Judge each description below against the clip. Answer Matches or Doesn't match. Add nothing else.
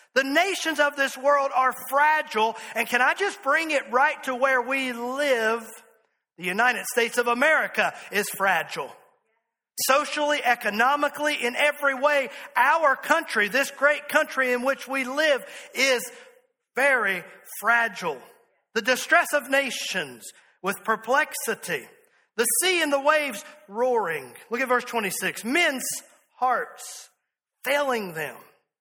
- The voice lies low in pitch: Doesn't match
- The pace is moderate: Doesn't match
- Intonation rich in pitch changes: Doesn't match